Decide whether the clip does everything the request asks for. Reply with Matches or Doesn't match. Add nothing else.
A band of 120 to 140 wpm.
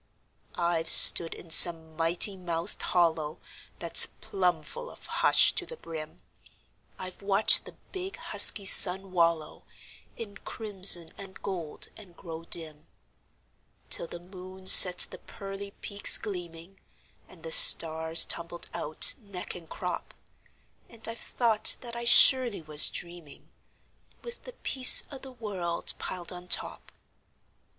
Matches